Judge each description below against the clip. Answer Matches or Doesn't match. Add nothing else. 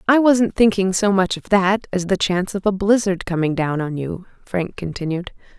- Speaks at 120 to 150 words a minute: Doesn't match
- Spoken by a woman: Matches